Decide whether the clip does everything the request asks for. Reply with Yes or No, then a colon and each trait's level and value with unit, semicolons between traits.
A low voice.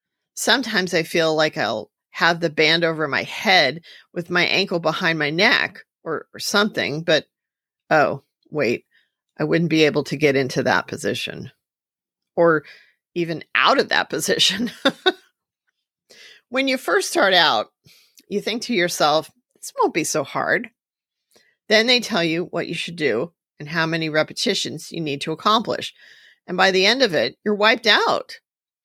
No: medium, 175 Hz